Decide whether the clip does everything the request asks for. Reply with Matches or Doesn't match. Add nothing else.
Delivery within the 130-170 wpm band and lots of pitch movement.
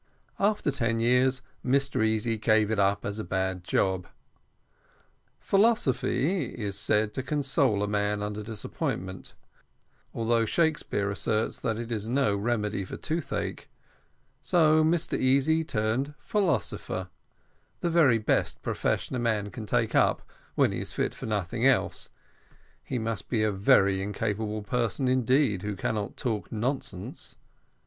Doesn't match